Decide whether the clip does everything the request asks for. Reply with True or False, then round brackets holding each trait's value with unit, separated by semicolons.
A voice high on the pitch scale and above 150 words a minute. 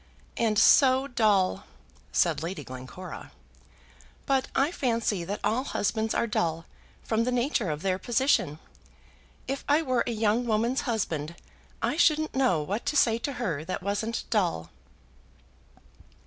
False (220 Hz; 140 wpm)